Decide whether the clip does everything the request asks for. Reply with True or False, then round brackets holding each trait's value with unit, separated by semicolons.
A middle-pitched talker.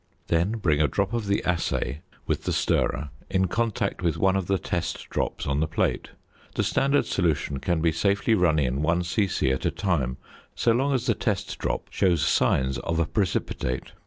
False (90 Hz)